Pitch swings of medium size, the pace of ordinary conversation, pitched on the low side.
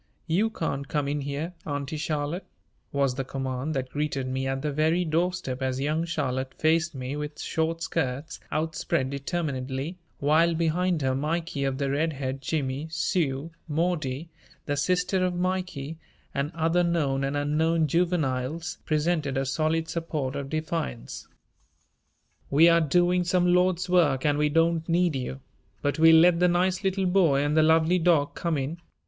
No: average, 3.5 semitones; average, 160 wpm; medium, 155 Hz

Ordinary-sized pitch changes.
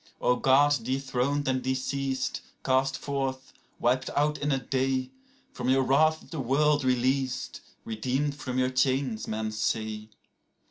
No: narrow, 1.7 semitones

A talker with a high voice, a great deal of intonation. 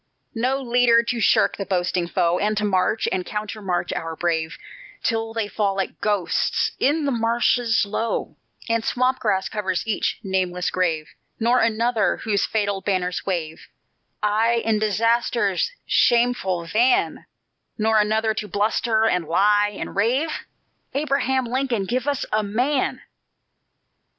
No: high, 215 Hz; average, 3.6 semitones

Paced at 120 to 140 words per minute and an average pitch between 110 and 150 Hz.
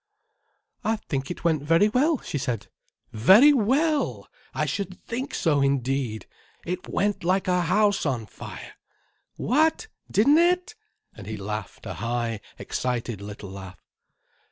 No: slow, 135 wpm; medium, 170 Hz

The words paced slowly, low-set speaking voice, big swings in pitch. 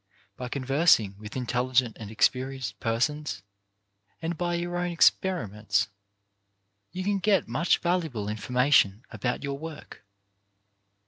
Yes: slow, 120 wpm; low, 130 Hz; wide, 7.1 semitones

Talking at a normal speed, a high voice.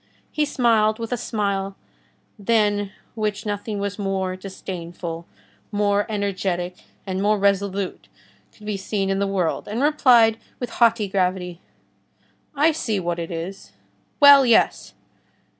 No: slow, 125 wpm; high, 200 Hz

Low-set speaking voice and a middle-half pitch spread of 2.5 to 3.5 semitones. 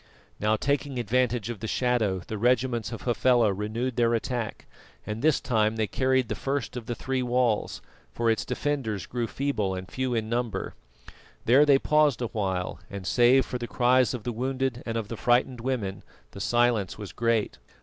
Yes: low, 120 Hz; average, 2.8 semitones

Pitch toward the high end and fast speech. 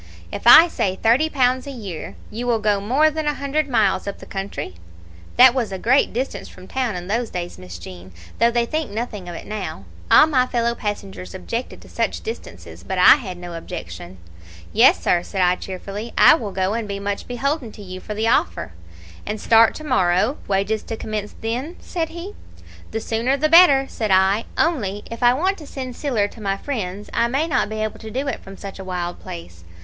Yes: high, 220 Hz; fast, 215 wpm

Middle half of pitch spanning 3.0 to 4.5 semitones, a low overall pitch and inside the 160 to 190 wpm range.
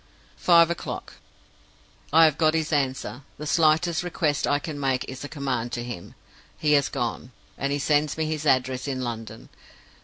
No: average, 3.4 semitones; medium, 145 Hz; average, 175 wpm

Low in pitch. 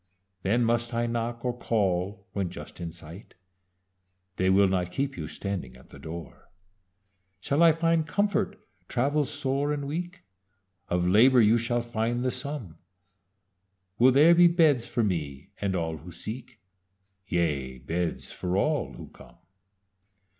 Yes: low, 115 Hz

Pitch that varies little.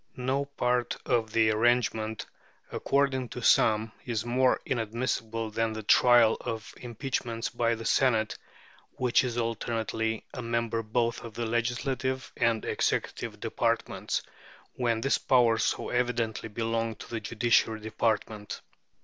Yes: narrow, 1.7 semitones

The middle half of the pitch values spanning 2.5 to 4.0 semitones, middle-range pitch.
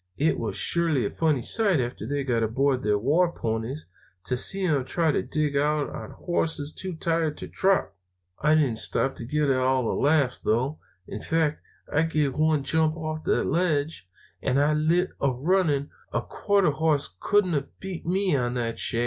Yes: average, 3.7 semitones; medium, 150 Hz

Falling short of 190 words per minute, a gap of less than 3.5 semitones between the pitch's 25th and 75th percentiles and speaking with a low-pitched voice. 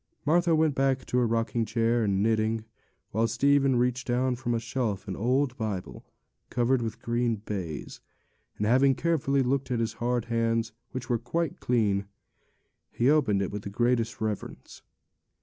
Yes: average, 160 wpm; average, 2.9 semitones; low, 120 Hz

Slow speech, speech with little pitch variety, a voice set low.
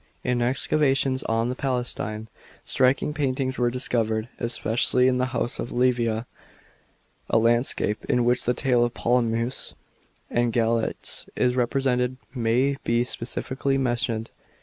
Yes: slow, 125 wpm; narrow, 1.8 semitones; low, 125 Hz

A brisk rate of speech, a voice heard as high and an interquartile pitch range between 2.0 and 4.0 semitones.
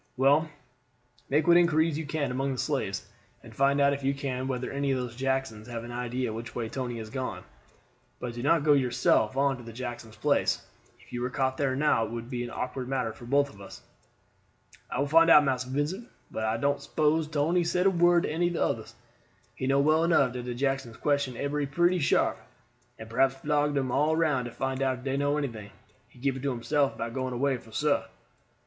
No: fast, 225 wpm; low, 135 Hz; average, 3.0 semitones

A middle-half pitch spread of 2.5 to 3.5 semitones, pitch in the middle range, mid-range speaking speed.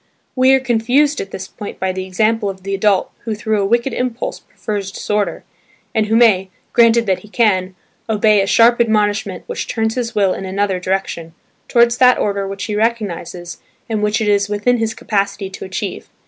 No: average, 2.9 semitones; high, 210 Hz; average, 190 wpm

